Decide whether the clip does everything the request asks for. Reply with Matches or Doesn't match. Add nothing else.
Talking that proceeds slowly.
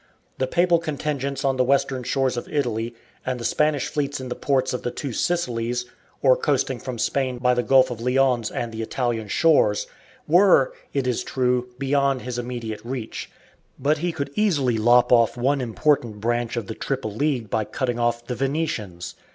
Doesn't match